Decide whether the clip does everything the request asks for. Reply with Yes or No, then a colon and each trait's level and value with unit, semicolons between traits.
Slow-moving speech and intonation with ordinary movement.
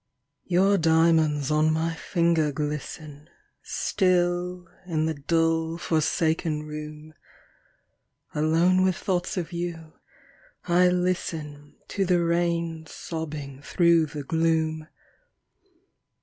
No: slow, 95 wpm; narrow, 2.2 semitones